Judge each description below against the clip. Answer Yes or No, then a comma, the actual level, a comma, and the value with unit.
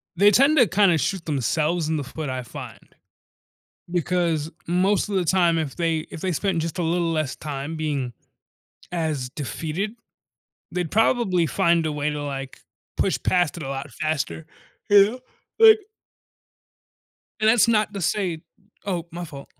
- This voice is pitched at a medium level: Yes, medium, 165 Hz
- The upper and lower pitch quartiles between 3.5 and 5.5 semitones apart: Yes, average, 4.1 semitones